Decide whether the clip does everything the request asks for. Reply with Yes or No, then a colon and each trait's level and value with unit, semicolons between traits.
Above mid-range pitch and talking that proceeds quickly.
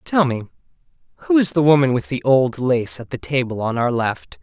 No: low, 130 Hz; fast, 215 wpm